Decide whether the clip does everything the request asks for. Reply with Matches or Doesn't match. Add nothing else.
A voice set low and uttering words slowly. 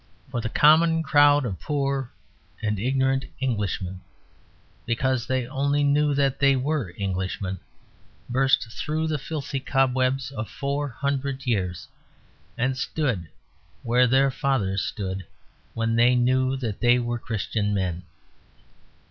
Matches